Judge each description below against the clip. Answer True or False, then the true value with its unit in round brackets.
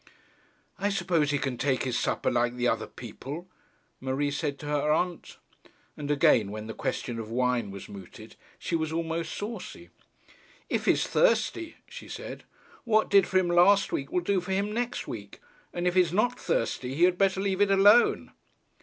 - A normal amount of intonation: False (6.8 semitones)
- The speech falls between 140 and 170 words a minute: False (180 wpm)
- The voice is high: False (165 Hz)